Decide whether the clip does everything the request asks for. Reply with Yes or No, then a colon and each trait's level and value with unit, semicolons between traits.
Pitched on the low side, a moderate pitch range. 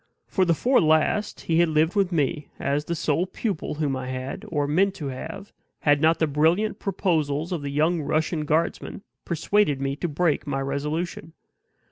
No: medium, 160 Hz; average, 3.2 semitones